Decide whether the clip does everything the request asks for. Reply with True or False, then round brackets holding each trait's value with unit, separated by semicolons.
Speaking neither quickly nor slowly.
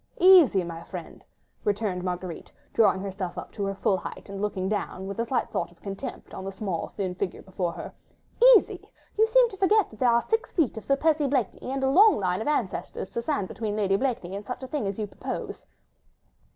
False (215 wpm)